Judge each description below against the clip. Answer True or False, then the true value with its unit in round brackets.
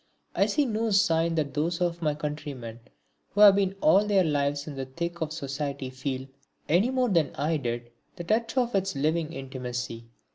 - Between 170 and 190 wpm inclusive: True (185 wpm)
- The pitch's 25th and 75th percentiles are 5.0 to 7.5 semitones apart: True (5.6 semitones)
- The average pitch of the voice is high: False (155 Hz)